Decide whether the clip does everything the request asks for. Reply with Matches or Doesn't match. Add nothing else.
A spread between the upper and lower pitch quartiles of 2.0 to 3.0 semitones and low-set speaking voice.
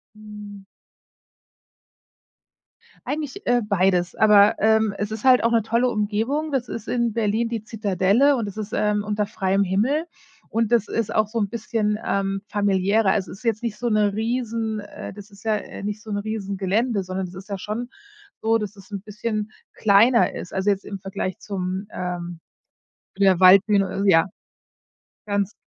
Doesn't match